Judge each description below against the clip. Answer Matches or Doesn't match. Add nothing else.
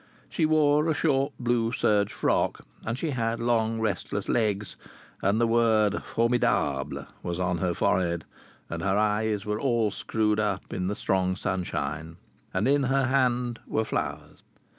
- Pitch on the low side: Matches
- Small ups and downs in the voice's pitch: Doesn't match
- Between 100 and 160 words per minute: Matches